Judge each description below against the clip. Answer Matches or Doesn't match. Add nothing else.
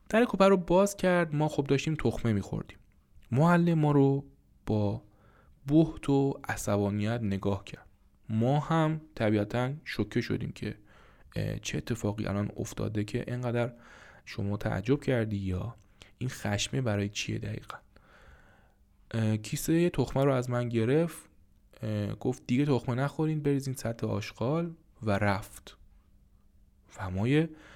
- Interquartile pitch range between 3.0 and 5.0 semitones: Doesn't match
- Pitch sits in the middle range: Doesn't match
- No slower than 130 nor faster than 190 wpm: Doesn't match